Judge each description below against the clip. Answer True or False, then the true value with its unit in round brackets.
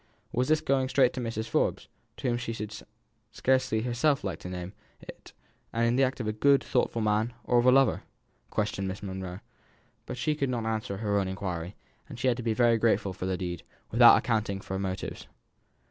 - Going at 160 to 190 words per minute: False (205 wpm)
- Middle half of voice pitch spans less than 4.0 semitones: False (4.4 semitones)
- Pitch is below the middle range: True (110 Hz)